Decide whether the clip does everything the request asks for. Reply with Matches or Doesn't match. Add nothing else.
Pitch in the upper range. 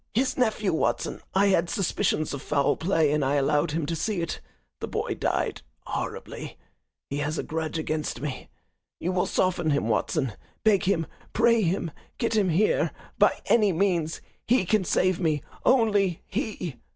Doesn't match